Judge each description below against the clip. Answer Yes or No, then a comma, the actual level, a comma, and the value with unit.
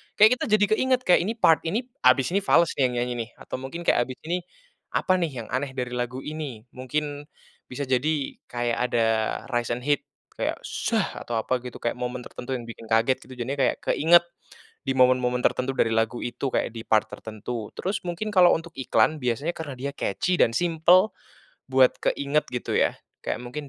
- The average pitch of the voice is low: Yes, low, 130 Hz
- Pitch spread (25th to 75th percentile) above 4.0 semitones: Yes, average, 4.8 semitones